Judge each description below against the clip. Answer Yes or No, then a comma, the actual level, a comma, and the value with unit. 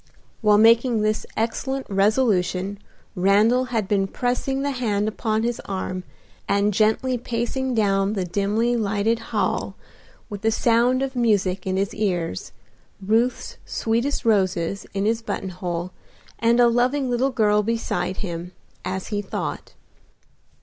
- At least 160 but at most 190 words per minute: No, slow, 135 wpm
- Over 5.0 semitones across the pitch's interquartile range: No, average, 3.3 semitones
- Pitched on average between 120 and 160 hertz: No, high, 215 Hz